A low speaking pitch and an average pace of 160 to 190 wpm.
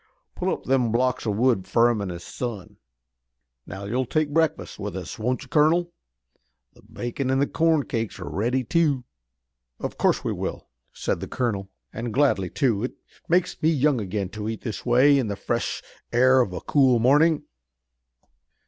Yes: low, 125 Hz; average, 180 wpm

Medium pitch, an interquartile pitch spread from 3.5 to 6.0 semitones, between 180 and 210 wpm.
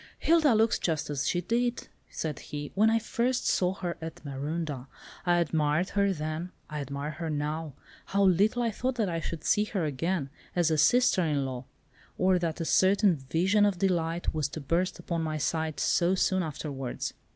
Yes: medium, 170 Hz; average, 4.3 semitones; average, 185 wpm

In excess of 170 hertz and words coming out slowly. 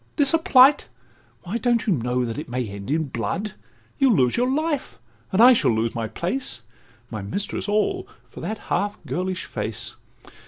No: high, 190 Hz; average, 180 wpm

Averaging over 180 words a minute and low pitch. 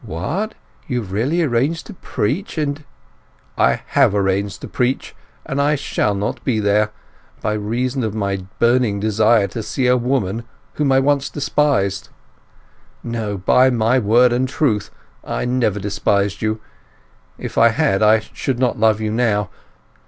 No: average, 150 wpm; low, 115 Hz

